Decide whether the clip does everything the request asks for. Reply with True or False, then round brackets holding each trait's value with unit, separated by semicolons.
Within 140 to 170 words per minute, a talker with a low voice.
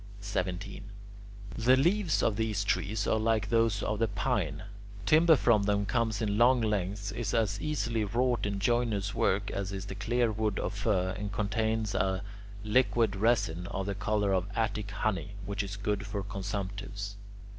True (165 wpm; 105 Hz)